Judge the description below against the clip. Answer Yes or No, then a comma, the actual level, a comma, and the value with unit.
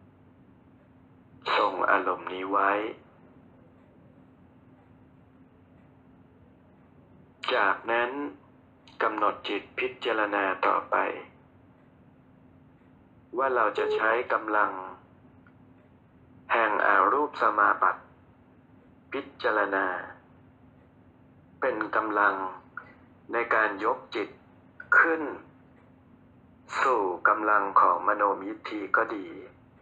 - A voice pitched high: Yes, very high, 330 Hz